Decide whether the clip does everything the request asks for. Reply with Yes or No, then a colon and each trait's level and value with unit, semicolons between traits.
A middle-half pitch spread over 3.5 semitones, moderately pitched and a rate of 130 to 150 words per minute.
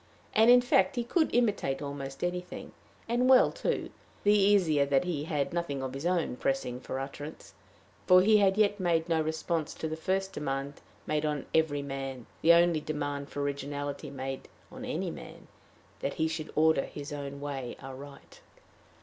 No: average, 4.3 semitones; medium, 155 Hz; average, 175 wpm